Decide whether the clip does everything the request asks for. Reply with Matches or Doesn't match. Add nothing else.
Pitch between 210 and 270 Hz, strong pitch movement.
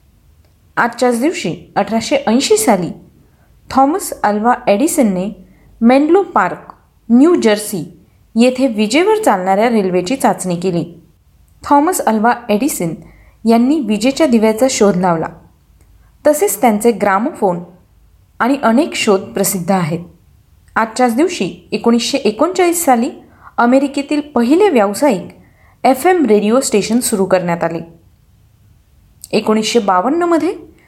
Matches